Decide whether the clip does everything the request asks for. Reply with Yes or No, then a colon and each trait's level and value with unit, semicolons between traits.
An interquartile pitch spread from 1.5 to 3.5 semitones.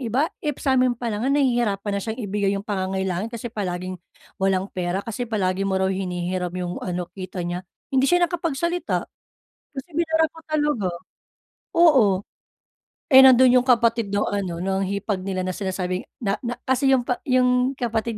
No: wide, 5.4 semitones